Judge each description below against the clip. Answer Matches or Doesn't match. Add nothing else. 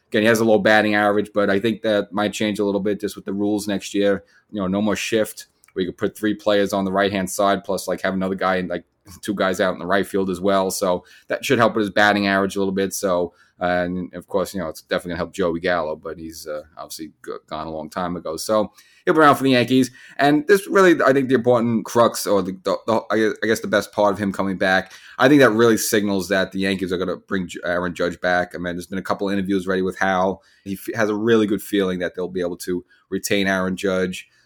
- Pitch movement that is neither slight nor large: Doesn't match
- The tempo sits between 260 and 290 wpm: Matches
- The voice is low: Matches